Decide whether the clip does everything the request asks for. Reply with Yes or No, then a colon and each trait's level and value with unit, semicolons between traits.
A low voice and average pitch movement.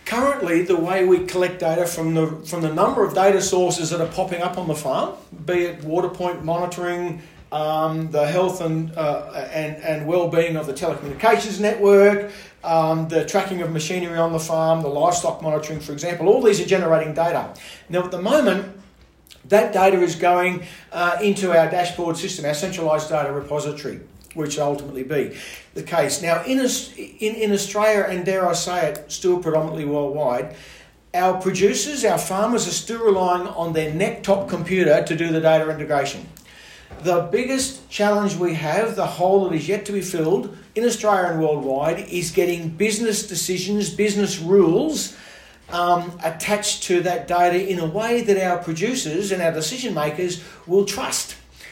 No: medium, 175 Hz; average, 3.4 semitones